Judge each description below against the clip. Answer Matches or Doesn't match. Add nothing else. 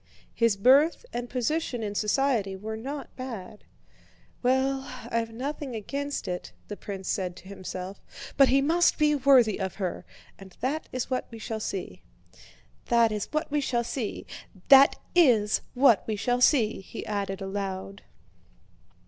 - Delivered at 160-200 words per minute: Doesn't match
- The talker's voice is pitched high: Matches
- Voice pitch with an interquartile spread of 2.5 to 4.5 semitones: Doesn't match